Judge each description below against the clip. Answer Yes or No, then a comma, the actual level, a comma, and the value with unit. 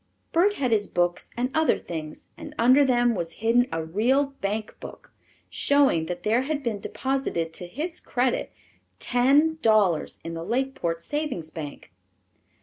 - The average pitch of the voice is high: Yes, high, 235 Hz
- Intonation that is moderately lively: No, wide, 7.8 semitones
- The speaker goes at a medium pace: Yes, average, 150 wpm